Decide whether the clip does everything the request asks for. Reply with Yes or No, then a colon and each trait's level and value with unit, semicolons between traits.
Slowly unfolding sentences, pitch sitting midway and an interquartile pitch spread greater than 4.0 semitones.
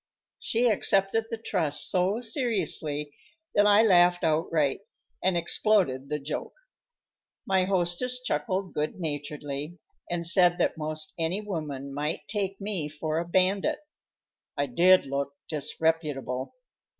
Yes: slow, 125 wpm; medium, 170 Hz; average, 4.7 semitones